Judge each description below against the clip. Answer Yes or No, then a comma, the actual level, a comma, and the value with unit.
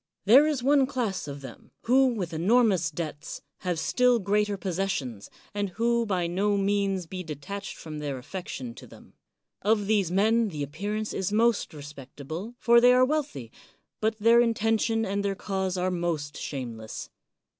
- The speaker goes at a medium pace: Yes, average, 170 wpm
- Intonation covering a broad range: Yes, wide, 5.8 semitones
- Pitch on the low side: No, high, 195 Hz